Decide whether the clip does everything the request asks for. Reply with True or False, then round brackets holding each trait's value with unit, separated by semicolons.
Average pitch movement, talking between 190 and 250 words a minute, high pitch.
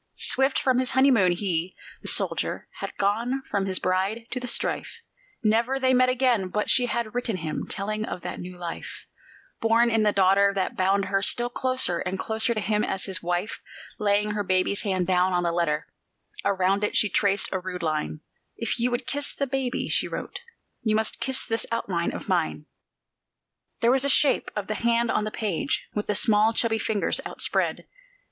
True (4.1 semitones; 195 wpm; 210 Hz)